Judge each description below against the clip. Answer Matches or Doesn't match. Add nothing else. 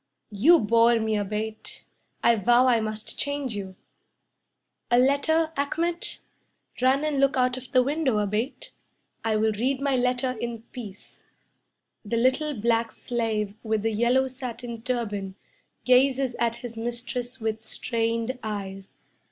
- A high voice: Matches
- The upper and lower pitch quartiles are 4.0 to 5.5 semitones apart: Doesn't match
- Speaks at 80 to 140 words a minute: Matches